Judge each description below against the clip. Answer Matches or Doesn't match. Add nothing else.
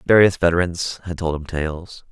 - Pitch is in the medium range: Doesn't match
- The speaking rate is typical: Matches